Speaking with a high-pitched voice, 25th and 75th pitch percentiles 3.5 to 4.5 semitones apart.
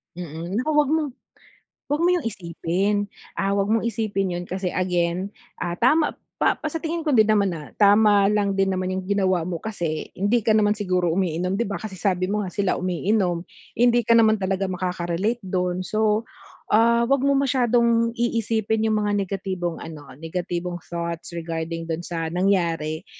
Yes: high, 195 Hz; average, 3.9 semitones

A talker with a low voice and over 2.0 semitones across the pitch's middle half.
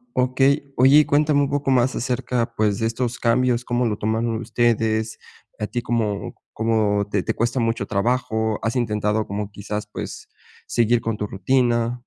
Yes: low, 115 Hz; narrow, 2.6 semitones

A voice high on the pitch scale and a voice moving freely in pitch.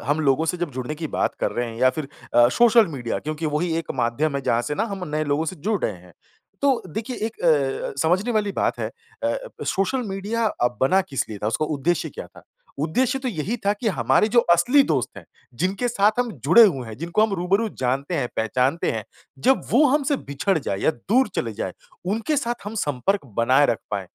No: medium, 170 Hz; wide, 8.0 semitones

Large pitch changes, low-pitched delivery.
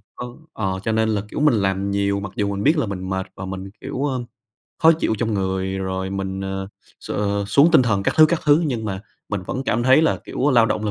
No: average, 5.0 semitones; low, 100 Hz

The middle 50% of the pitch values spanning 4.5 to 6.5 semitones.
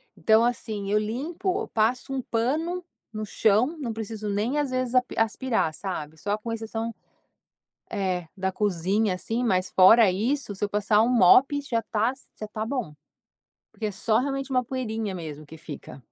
No: average, 4.0 semitones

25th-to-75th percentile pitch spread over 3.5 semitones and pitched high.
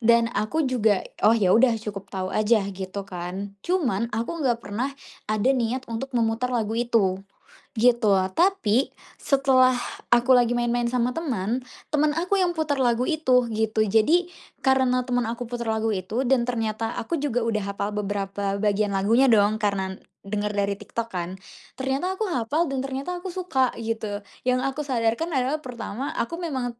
Yes: average, 3.9 semitones; high, 235 Hz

